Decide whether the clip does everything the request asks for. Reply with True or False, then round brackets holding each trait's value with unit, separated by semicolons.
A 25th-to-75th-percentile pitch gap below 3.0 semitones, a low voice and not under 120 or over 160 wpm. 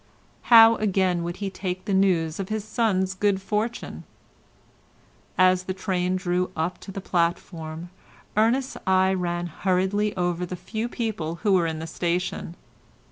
False (2.6 semitones; 185 Hz; 150 wpm)